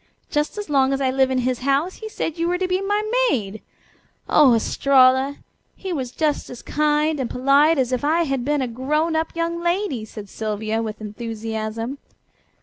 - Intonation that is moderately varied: Yes, average, 4.9 semitones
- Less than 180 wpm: No, average, 190 wpm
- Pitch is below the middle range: No, very high, 275 Hz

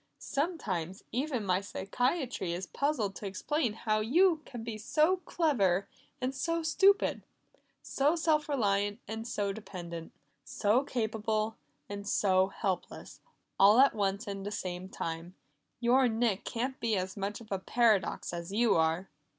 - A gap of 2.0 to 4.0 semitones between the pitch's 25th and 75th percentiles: No, average, 5.2 semitones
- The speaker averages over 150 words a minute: No, average, 145 wpm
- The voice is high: Yes, high, 215 Hz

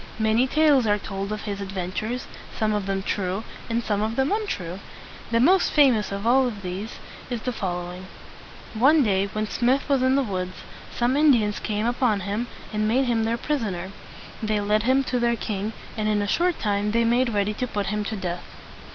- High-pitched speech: Yes, high, 215 Hz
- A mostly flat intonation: No, average, 3.7 semitones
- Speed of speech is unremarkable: No, fast, 215 wpm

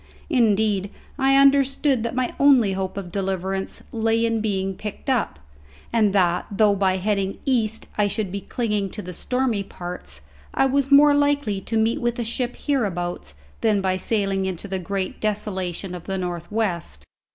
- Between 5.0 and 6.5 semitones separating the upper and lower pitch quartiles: No, average, 3.9 semitones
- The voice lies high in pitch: Yes, high, 205 Hz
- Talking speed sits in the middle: Yes, average, 170 wpm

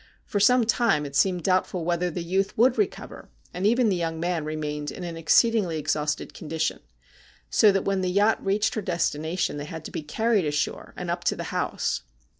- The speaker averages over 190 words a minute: Yes, average, 200 wpm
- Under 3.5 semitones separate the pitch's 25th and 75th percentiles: No, average, 4.3 semitones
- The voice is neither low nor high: Yes, medium, 180 Hz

